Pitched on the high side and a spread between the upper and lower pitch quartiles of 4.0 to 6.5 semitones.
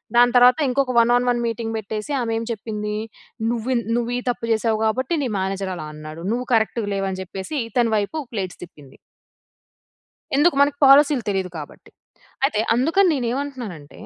Yes: high, 230 Hz; average, 4.3 semitones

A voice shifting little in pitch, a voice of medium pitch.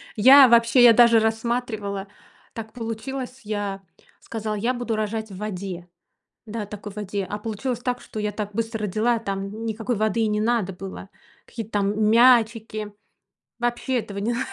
No: narrow, 2.3 semitones; high, 220 Hz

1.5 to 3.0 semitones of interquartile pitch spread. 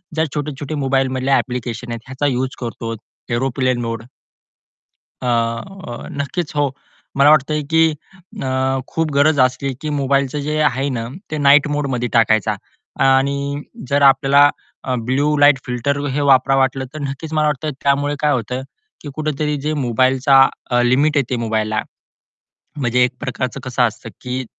Yes: narrow, 2.5 semitones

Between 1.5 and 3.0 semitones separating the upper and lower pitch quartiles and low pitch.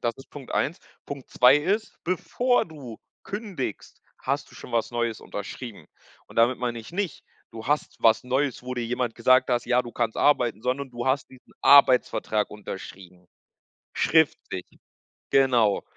No: average, 3.5 semitones; low, 125 Hz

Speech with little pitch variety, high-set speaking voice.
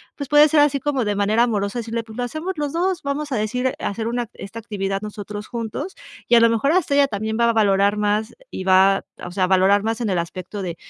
No: average, 4.6 semitones; high, 225 Hz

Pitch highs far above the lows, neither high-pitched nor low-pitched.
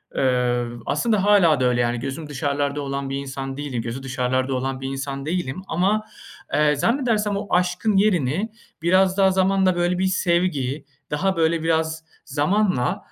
Yes: wide, 5.8 semitones; medium, 150 Hz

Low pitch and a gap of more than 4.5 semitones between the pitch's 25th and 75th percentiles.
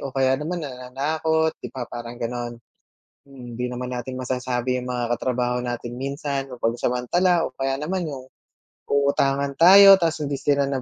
No: low, 130 Hz; narrow, 2.6 semitones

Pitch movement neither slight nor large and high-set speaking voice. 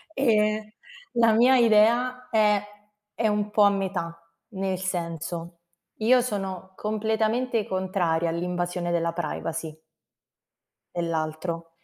Yes: average, 4.3 semitones; high, 195 Hz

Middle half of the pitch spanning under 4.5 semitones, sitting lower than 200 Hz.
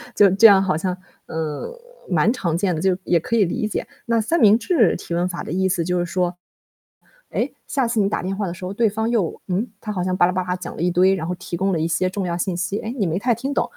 Yes: average, 3.2 semitones; medium, 185 Hz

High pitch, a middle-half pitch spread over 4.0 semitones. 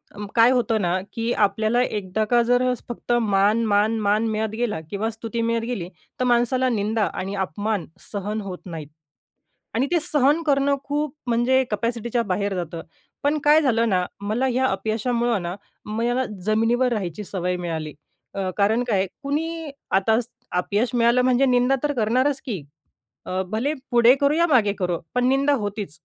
No: high, 230 Hz; average, 3.7 semitones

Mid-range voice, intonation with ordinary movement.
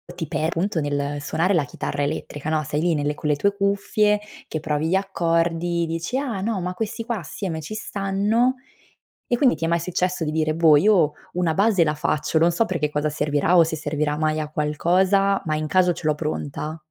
Yes: medium, 165 Hz; average, 4.2 semitones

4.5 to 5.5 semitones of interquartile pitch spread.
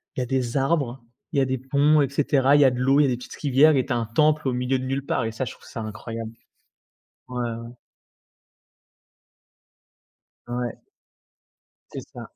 No: narrow, 2.6 semitones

